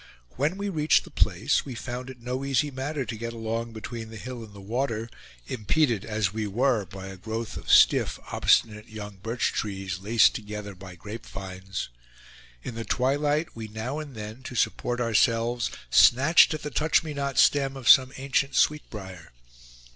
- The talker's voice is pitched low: Yes, low, 115 Hz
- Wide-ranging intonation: No, average, 4.3 semitones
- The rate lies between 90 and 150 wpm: No, average, 175 wpm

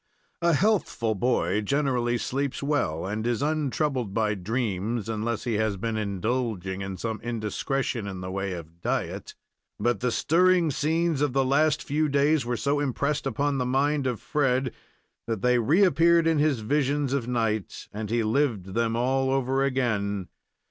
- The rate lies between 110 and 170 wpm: Yes, average, 160 wpm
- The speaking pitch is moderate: No, low, 125 Hz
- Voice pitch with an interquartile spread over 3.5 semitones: Yes, average, 4.7 semitones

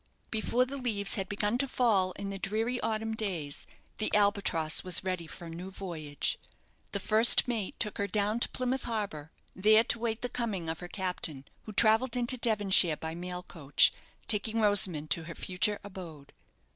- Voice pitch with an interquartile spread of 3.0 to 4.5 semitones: Yes, average, 4.0 semitones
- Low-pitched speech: No, high, 200 Hz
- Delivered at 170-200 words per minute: Yes, average, 180 wpm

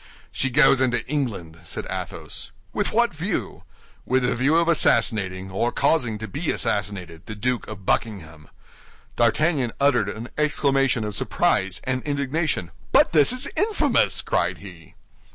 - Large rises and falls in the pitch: Yes, wide, 5.9 semitones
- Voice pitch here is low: Yes, low, 120 Hz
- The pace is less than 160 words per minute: Yes, average, 145 wpm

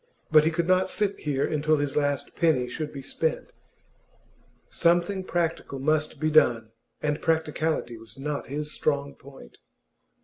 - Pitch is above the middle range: No, medium, 150 Hz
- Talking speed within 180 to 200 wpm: No, average, 145 wpm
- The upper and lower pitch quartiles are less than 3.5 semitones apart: Yes, narrow, 2.6 semitones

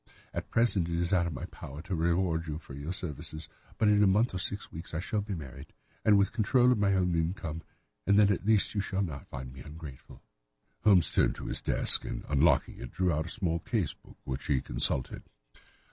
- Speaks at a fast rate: Yes, fast, 220 wpm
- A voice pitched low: Yes, very low, 85 Hz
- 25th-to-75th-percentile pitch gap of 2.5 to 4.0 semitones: No, average, 4.6 semitones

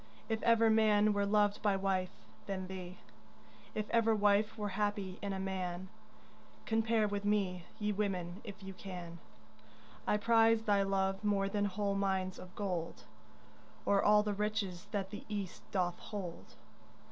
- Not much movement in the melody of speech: Yes, narrow, 1.8 semitones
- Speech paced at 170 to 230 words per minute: No, average, 155 wpm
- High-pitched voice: Yes, high, 200 Hz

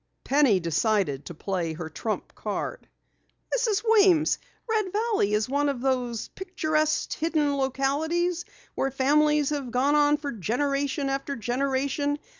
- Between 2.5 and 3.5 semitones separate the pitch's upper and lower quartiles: No, average, 4.2 semitones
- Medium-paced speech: No, slow, 130 wpm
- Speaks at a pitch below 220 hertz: No, very high, 280 Hz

